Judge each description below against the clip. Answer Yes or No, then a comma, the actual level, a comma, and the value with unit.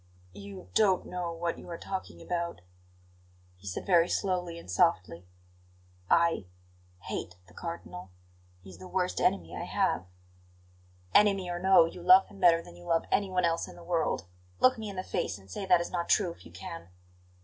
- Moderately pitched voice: Yes, medium, 170 Hz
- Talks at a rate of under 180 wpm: No, average, 185 wpm